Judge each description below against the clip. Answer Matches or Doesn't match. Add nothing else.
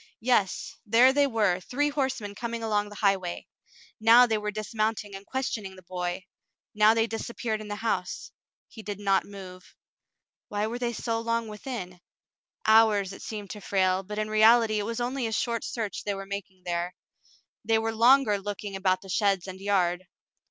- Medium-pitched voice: Doesn't match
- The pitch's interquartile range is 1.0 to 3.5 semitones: Matches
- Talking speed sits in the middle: Matches